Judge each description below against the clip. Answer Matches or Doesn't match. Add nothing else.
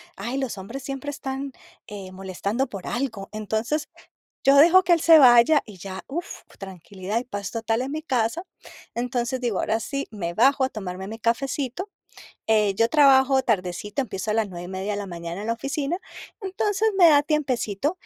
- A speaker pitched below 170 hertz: Doesn't match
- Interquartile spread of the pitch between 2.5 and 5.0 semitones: Doesn't match